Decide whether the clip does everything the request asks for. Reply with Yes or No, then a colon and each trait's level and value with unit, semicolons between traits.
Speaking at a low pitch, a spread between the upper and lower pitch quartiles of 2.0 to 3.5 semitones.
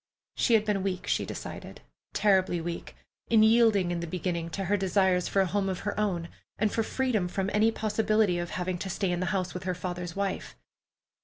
No: high, 190 Hz; average, 2.9 semitones